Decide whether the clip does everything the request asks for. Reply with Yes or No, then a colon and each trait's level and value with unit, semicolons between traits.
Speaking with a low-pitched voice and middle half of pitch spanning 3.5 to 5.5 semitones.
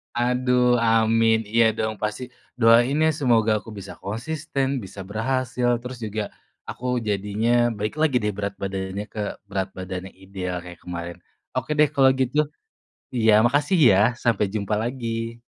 Yes: low, 115 Hz; average, 3.8 semitones